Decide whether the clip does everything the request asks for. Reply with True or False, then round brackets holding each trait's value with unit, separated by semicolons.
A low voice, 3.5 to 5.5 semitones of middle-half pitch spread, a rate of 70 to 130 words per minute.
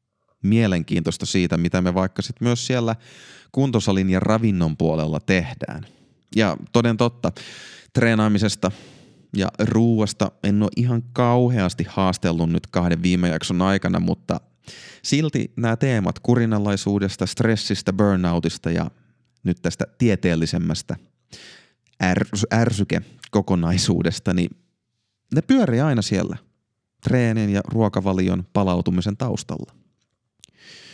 True (105 Hz; 3.9 semitones; 100 wpm)